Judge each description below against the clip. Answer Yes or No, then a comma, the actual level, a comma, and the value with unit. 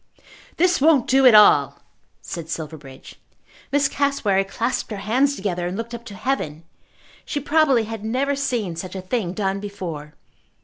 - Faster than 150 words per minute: Yes, average, 160 wpm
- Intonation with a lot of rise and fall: Yes, wide, 6.6 semitones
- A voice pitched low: No, high, 215 Hz